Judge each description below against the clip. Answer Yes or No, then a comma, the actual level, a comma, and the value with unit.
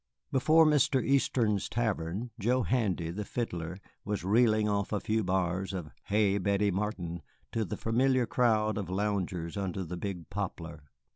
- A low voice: Yes, low, 100 Hz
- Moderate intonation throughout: Yes, average, 3.7 semitones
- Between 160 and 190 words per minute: No, average, 150 wpm